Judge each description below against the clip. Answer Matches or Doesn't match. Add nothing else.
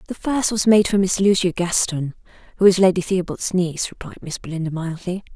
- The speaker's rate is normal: Matches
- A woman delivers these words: Matches